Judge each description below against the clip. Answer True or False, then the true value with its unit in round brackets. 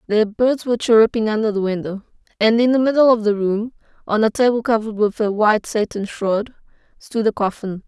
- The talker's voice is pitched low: False (220 Hz)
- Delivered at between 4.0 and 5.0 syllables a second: False (5.8 syllables/s)